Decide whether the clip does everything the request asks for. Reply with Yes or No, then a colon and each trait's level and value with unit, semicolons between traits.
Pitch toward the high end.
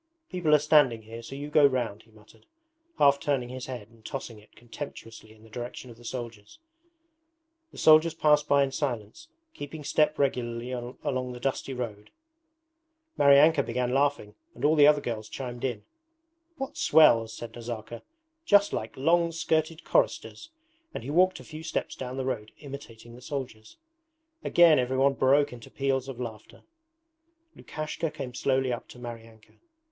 No: low, 130 Hz